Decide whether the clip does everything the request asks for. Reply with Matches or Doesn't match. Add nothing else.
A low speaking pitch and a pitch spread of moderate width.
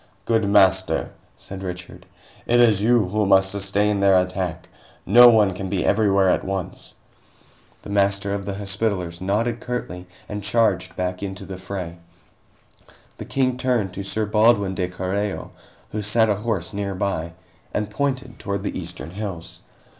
Doesn't match